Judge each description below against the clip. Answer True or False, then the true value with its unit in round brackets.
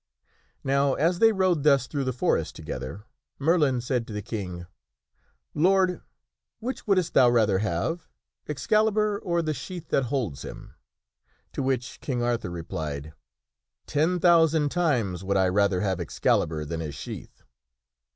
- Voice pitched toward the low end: True (130 Hz)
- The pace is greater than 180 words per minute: False (145 wpm)